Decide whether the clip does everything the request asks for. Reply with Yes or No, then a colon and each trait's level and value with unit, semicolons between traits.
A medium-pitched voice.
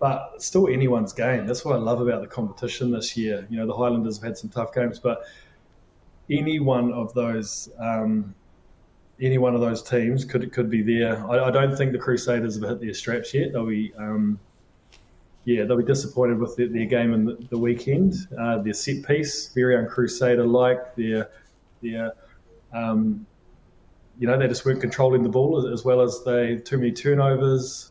No: low, 120 Hz